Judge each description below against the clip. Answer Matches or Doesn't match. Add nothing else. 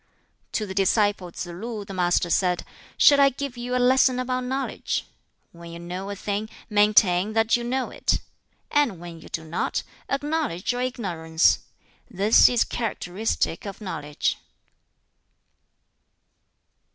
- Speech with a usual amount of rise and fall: Doesn't match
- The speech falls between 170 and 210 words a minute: Doesn't match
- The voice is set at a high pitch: Matches